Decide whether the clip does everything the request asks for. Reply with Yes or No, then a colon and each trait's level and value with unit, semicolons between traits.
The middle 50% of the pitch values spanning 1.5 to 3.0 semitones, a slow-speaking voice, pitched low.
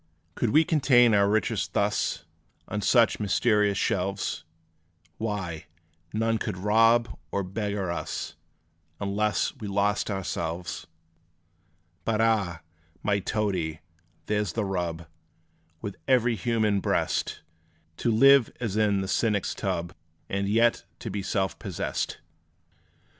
Yes: average, 2.7 semitones; slow, 115 wpm; low, 105 Hz